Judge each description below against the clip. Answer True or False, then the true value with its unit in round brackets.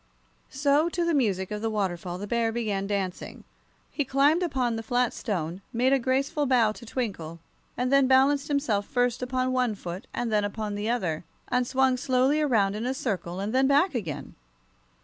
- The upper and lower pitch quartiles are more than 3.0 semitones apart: True (4.5 semitones)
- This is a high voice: True (245 Hz)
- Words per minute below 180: False (190 wpm)